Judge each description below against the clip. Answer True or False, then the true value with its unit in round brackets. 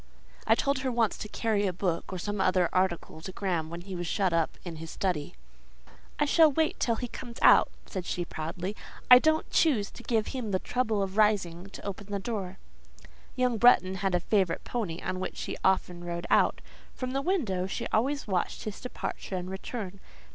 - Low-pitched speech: False (195 Hz)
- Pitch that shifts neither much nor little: True (4.6 semitones)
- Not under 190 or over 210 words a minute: True (200 wpm)